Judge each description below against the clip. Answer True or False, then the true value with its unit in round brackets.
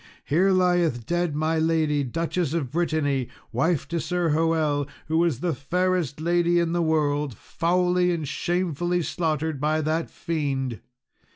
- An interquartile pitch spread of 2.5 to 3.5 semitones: True (2.9 semitones)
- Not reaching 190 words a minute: True (145 wpm)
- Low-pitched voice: False (160 Hz)